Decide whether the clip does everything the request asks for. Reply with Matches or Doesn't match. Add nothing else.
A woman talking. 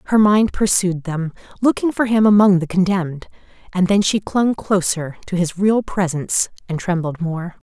Matches